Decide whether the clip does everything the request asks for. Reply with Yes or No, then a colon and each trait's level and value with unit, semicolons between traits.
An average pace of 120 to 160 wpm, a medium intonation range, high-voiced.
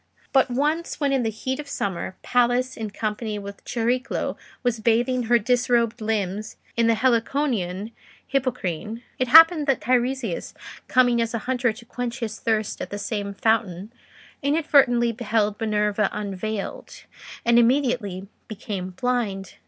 Yes: average, 140 wpm; average, 3.2 semitones; high, 230 Hz